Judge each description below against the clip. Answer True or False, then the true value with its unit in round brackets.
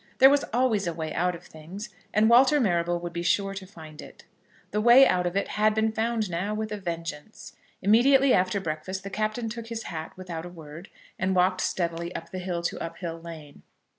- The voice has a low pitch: False (190 Hz)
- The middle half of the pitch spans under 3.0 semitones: False (4.3 semitones)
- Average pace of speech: False (210 wpm)